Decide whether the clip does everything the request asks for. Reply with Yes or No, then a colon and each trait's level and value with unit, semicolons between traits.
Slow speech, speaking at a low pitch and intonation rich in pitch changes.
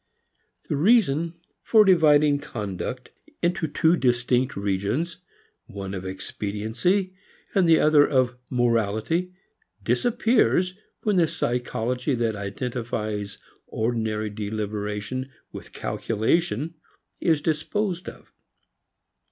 Yes: slow, 95 wpm; low, 125 Hz; wide, 7.4 semitones